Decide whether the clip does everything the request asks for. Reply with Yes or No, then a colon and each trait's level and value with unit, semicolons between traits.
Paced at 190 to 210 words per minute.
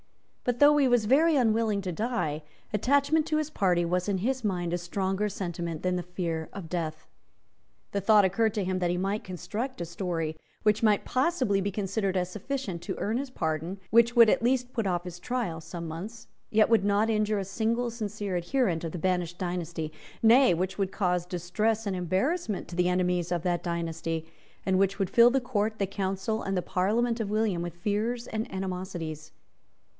Yes: average, 200 wpm